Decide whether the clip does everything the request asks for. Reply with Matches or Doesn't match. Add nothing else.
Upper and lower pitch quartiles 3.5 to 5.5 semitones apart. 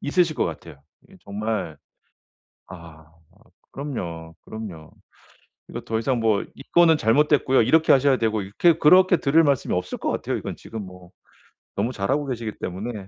Doesn't match